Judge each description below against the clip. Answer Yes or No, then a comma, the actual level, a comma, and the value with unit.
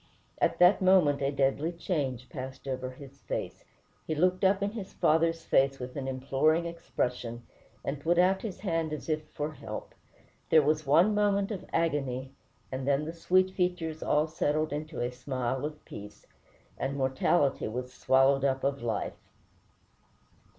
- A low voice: No, medium, 150 Hz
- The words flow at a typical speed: Yes, average, 160 wpm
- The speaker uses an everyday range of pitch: Yes, average, 4.1 semitones